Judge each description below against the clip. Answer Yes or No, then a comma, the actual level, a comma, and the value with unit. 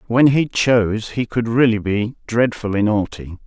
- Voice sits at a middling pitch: No, low, 110 Hz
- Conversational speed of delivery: Yes, average, 155 wpm